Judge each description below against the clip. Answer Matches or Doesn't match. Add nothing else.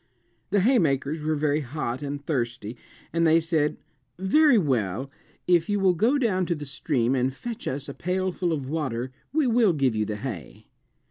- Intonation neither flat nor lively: Doesn't match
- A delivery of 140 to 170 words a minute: Doesn't match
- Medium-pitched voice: Matches